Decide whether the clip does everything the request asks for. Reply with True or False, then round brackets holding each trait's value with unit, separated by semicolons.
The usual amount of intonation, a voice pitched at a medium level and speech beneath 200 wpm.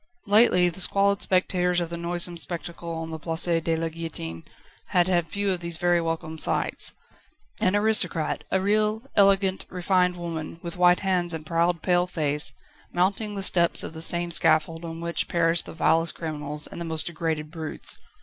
False (1.9 semitones; 170 Hz; 175 wpm)